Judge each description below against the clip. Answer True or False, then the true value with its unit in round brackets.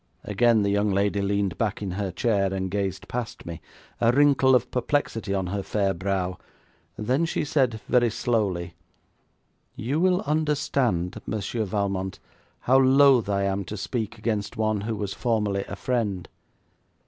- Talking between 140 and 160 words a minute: True (155 wpm)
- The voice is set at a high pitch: False (105 Hz)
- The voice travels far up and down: False (3.8 semitones)